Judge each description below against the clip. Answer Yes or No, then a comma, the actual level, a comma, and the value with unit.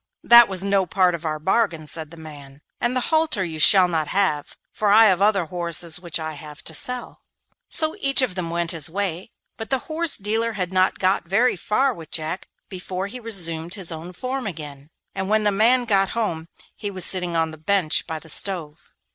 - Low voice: No, medium, 185 Hz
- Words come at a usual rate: No, fast, 215 wpm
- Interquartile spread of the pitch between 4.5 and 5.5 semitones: Yes, average, 4.8 semitones